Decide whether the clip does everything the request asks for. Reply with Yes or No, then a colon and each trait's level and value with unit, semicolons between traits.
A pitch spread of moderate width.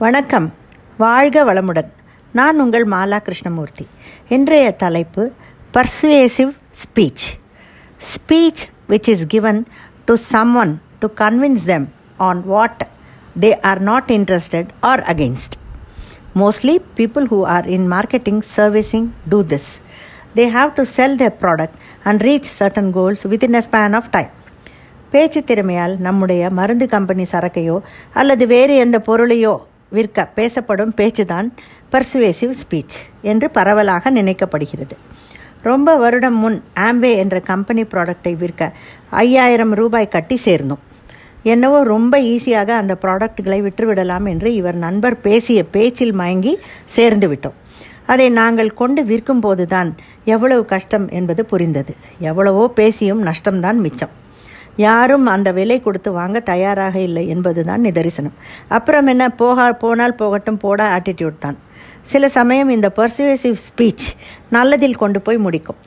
Yes: average, 4.7 semitones